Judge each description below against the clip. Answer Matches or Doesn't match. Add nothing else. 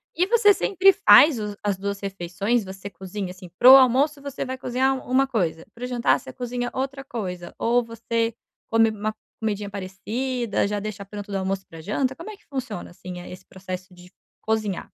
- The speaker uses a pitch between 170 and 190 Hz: Doesn't match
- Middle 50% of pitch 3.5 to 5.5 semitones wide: Matches